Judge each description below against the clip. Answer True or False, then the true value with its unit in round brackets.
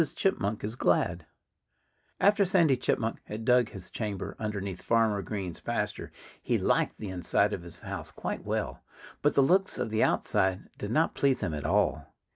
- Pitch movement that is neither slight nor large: False (5.7 semitones)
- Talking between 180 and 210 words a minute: False (170 wpm)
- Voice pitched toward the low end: True (110 Hz)